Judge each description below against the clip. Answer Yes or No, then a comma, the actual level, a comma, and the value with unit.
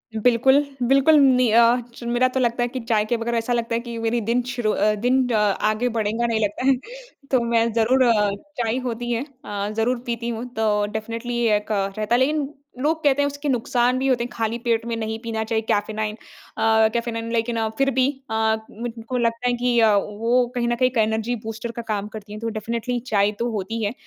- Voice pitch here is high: Yes, high, 230 Hz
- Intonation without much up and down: Yes, narrow, 1.9 semitones